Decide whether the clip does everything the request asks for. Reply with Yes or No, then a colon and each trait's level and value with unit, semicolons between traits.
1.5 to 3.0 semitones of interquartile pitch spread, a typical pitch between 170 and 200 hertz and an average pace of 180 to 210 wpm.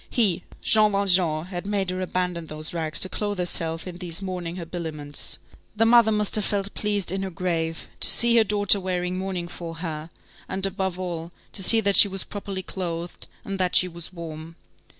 Yes: average, 2.7 semitones; medium, 185 Hz; average, 190 wpm